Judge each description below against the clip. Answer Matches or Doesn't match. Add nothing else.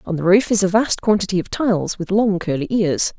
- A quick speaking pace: Matches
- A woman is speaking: Matches